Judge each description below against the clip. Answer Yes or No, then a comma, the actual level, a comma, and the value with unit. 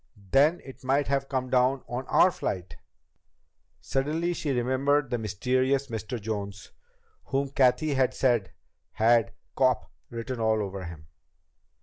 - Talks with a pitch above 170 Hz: No, low, 130 Hz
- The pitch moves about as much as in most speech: Yes, average, 3.7 semitones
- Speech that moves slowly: Yes, slow, 130 wpm